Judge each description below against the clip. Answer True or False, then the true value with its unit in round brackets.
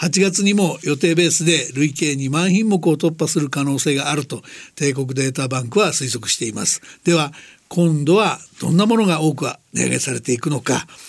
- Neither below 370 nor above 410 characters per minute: False (355 characters per minute)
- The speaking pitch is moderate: True (155 Hz)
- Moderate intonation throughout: True (4.1 semitones)